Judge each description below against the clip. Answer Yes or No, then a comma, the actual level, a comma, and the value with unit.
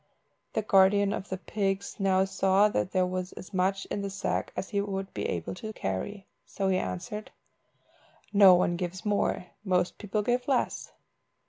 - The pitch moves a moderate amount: No, narrow, 1.7 semitones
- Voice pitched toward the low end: No, high, 195 Hz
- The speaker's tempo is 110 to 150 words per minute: No, average, 170 wpm